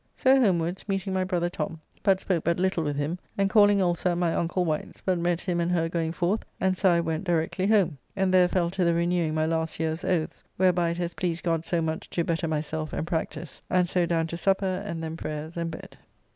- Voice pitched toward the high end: No, medium, 170 Hz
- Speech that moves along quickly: Yes, fast, 235 wpm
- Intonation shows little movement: Yes, narrow, 2.2 semitones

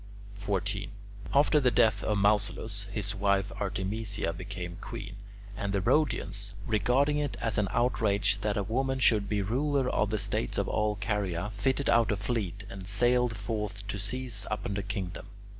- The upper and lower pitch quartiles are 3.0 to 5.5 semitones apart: No, narrow, 2.5 semitones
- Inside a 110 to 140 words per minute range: No, average, 165 wpm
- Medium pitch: No, low, 105 Hz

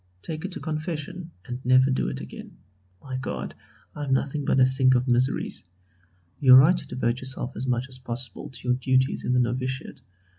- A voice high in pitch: No, low, 130 Hz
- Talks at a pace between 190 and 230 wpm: Yes, average, 200 wpm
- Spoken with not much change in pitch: Yes, narrow, 1.6 semitones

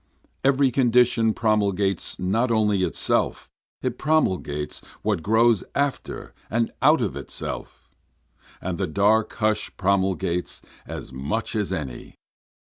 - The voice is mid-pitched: No, low, 105 Hz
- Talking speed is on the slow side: Yes, slow, 115 wpm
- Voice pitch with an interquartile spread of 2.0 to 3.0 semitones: No, average, 4.0 semitones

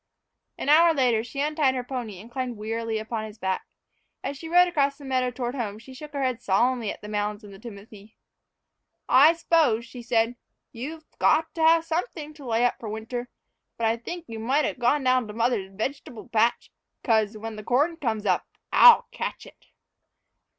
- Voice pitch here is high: Yes, high, 245 Hz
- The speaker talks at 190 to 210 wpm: Yes, average, 195 wpm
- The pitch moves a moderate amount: Yes, average, 4.4 semitones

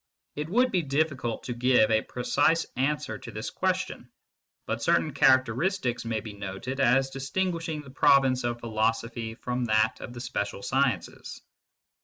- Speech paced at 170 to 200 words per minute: No, average, 150 wpm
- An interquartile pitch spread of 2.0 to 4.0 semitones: Yes, average, 3.7 semitones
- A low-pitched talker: Yes, low, 125 Hz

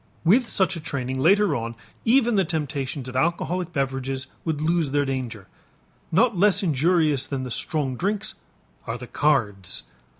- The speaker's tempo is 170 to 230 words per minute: No, average, 155 wpm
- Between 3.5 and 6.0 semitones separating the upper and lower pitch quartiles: Yes, wide, 5.5 semitones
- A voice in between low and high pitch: Yes, medium, 150 Hz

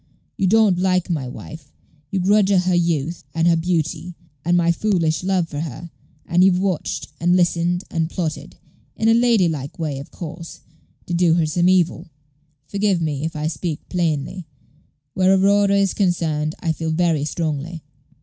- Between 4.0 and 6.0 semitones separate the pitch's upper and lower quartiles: No, narrow, 2.6 semitones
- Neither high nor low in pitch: Yes, medium, 175 Hz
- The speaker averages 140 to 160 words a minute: No, average, 170 wpm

